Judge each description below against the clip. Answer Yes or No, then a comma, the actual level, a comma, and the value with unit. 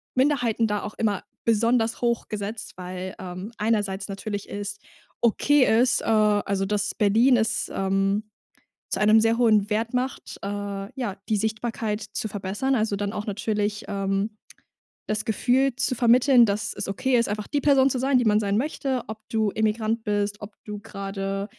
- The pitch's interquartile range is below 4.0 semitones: Yes, narrow, 2.5 semitones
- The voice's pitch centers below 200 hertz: No, high, 215 Hz